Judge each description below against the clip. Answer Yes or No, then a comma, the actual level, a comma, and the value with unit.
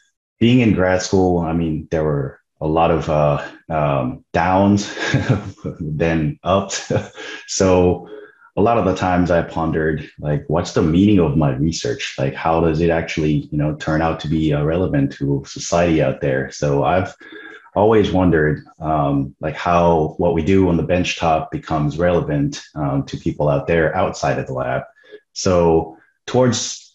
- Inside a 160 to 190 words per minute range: Yes, average, 165 wpm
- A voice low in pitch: Yes, very low, 85 Hz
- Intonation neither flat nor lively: Yes, average, 3.7 semitones